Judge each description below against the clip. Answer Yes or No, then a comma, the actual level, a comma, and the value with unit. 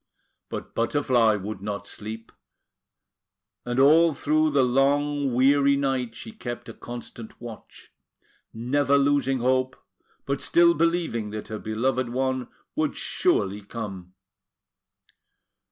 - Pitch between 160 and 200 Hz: No, low, 130 Hz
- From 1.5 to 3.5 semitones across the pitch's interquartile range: No, average, 4.0 semitones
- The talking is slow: Yes, slow, 115 wpm